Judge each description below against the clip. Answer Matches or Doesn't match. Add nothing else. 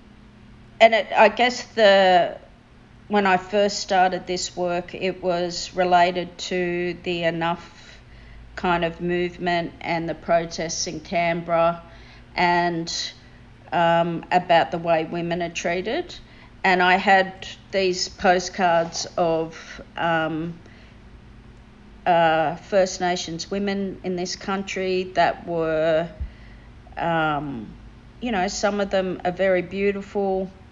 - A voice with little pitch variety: Matches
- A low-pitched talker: Doesn't match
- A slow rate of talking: Matches